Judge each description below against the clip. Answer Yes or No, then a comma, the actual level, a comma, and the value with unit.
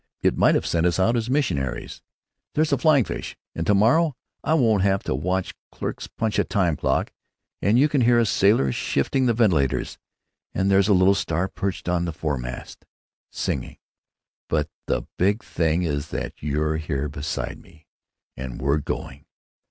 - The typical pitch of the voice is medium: No, very low, 95 Hz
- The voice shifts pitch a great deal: Yes, wide, 6.8 semitones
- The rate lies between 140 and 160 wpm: No, average, 175 wpm